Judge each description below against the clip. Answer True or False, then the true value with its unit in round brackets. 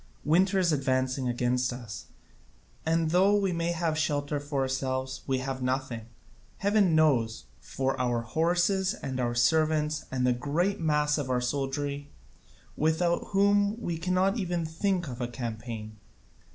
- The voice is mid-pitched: True (145 Hz)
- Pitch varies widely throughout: False (5.0 semitones)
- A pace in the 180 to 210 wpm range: False (145 wpm)